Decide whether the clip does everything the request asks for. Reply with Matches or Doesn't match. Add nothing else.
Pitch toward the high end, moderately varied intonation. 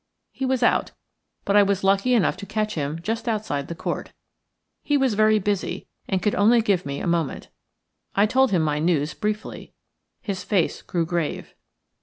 Matches